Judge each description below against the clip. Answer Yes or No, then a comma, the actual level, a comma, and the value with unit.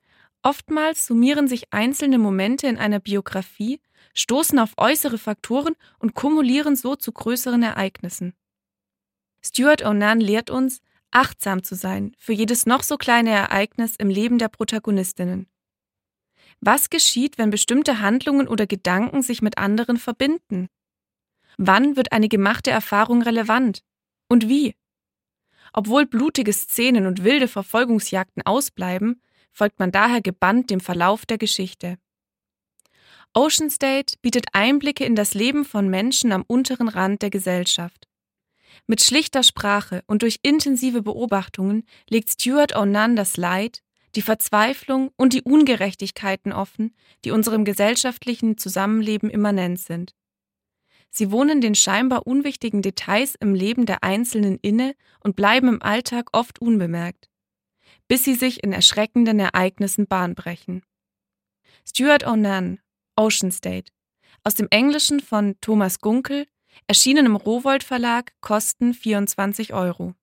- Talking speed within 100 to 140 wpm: Yes, slow, 125 wpm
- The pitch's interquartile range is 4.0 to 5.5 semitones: Yes, average, 4.3 semitones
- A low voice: No, high, 220 Hz